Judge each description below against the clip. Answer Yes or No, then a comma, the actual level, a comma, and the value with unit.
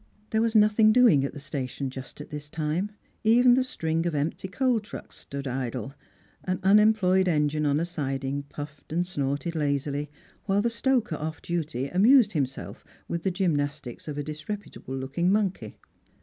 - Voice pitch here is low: No, medium, 160 Hz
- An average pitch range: No, wide, 6.2 semitones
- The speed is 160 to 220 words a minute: Yes, average, 165 wpm